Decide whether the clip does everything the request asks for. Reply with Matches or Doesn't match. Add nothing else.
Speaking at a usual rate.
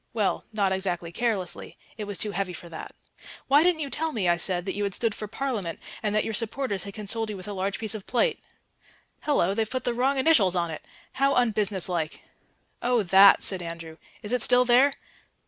Doesn't match